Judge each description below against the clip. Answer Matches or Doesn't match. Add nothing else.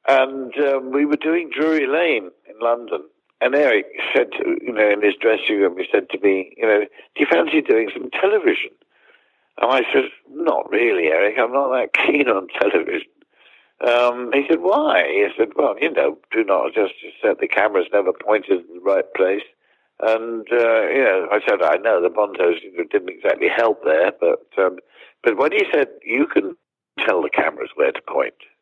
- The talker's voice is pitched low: Doesn't match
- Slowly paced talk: Doesn't match